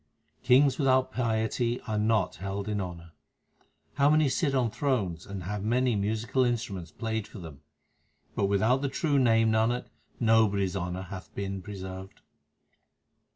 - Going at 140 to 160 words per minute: Yes, average, 155 wpm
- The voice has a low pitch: Yes, low, 110 Hz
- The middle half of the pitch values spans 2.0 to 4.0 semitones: No, average, 4.4 semitones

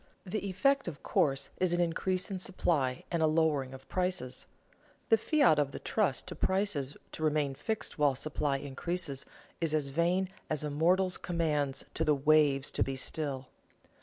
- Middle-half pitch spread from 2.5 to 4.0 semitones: No, average, 4.6 semitones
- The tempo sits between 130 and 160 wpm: No, average, 170 wpm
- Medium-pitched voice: Yes, medium, 155 Hz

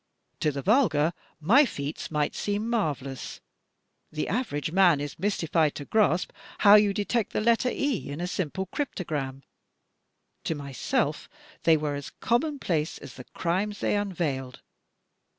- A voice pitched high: No, medium, 170 Hz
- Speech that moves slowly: No, average, 150 wpm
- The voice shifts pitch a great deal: Yes, wide, 6.1 semitones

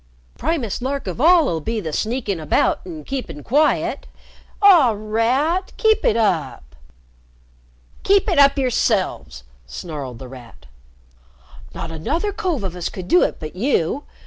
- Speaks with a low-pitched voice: No, high, 220 Hz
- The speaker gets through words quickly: No, average, 145 wpm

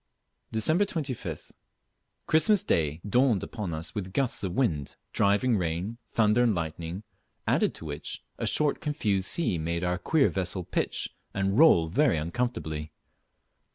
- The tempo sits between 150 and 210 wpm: No, slow, 135 wpm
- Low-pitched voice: Yes, low, 100 Hz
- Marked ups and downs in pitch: Yes, wide, 7.0 semitones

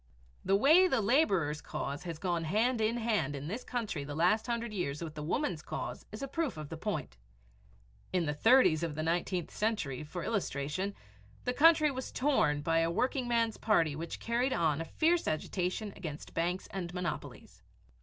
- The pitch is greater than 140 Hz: Yes, medium, 185 Hz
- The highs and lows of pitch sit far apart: Yes, wide, 6.9 semitones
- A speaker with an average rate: Yes, average, 180 wpm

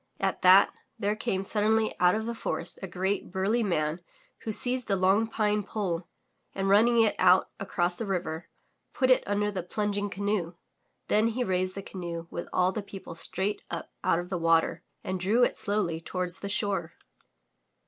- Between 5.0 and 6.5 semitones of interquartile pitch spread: No, average, 2.8 semitones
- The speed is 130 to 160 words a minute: No, average, 180 wpm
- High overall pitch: Yes, high, 195 Hz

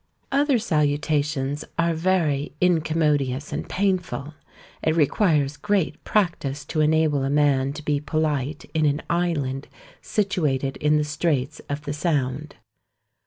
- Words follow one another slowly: Yes, slow, 125 wpm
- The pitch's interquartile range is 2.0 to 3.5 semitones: Yes, average, 2.7 semitones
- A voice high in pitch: No, medium, 150 Hz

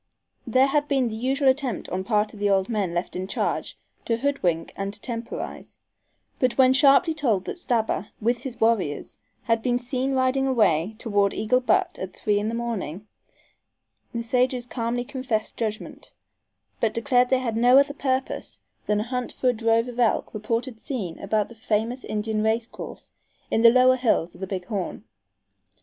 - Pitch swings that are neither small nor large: Yes, average, 3.3 semitones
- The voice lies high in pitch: Yes, high, 230 Hz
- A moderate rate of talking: Yes, average, 180 wpm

